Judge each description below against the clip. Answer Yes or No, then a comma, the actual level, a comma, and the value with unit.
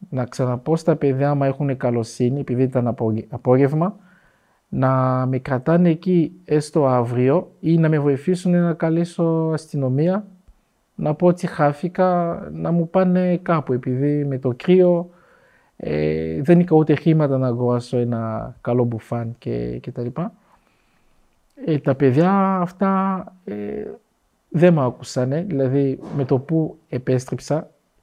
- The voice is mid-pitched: Yes, medium, 145 Hz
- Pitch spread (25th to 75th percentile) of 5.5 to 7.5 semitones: No, average, 5.1 semitones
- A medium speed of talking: Yes, average, 135 wpm